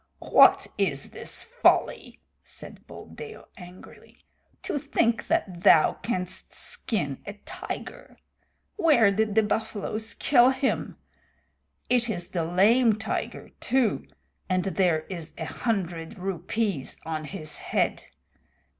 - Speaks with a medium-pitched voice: No, high, 200 Hz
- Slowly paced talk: Yes, slow, 115 wpm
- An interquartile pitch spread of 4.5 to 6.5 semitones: Yes, average, 5.1 semitones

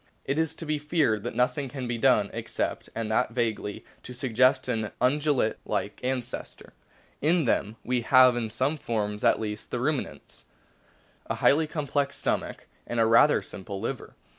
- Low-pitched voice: Yes, low, 125 Hz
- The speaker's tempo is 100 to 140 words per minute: No, average, 165 wpm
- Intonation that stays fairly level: No, average, 4.2 semitones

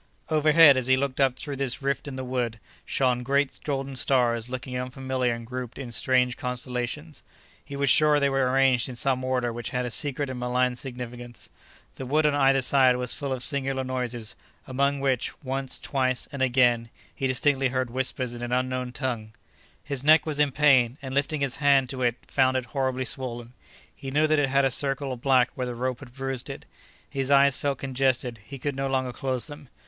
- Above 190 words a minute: Yes, average, 200 wpm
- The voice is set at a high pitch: No, low, 130 Hz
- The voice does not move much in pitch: Yes, narrow, 1.7 semitones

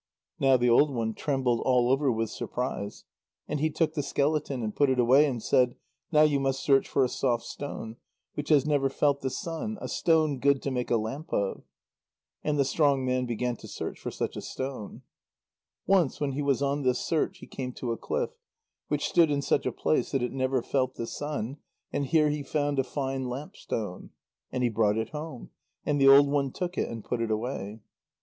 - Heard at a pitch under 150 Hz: Yes, low, 135 Hz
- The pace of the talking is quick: Yes, fast, 215 wpm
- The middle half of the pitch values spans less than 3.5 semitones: Yes, average, 2.9 semitones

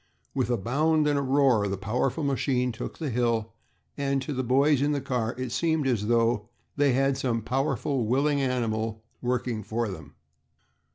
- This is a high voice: No, low, 125 Hz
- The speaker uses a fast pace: No, average, 175 wpm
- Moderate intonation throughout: Yes, average, 3.3 semitones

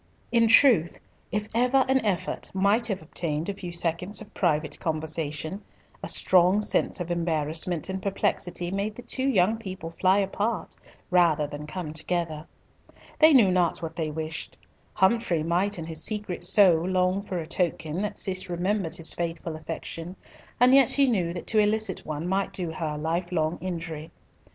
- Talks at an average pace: Yes, average, 170 wpm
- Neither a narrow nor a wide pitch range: Yes, average, 3.8 semitones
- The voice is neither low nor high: Yes, medium, 180 Hz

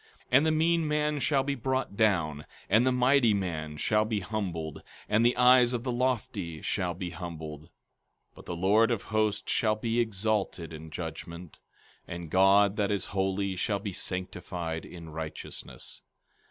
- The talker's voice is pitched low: Yes, low, 100 Hz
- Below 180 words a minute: Yes, average, 165 wpm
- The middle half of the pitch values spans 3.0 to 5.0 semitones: No, wide, 5.5 semitones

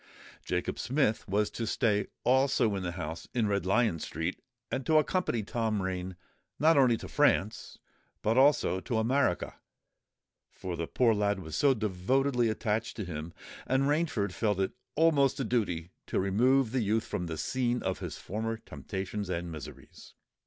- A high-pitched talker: No, low, 110 Hz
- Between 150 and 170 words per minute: Yes, average, 160 wpm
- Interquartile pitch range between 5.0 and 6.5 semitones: Yes, average, 5.3 semitones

